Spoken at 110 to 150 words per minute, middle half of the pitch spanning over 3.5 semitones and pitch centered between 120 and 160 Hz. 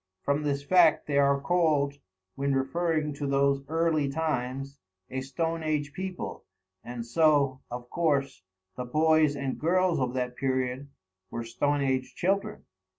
No: average, 145 wpm; average, 3.1 semitones; medium, 140 Hz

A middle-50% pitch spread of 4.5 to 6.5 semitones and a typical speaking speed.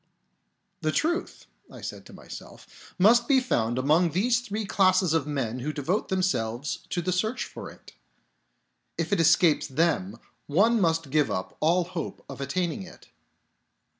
Yes: average, 5.0 semitones; average, 165 wpm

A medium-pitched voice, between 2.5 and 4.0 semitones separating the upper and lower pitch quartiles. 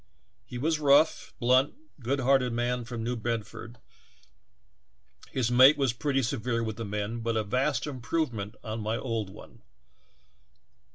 No: low, 120 Hz; average, 2.8 semitones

